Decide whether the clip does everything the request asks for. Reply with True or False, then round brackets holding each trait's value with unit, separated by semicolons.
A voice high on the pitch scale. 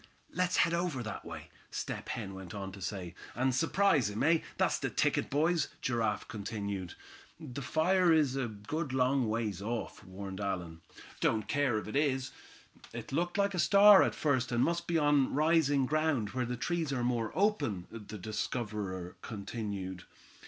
False (125 Hz)